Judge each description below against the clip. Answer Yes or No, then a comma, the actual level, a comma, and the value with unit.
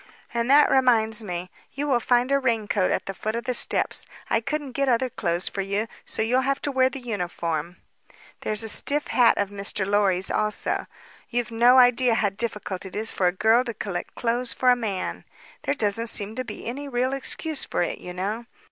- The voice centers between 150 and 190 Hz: No, high, 230 Hz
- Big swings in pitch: No, average, 3.9 semitones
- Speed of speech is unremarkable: No, fast, 210 wpm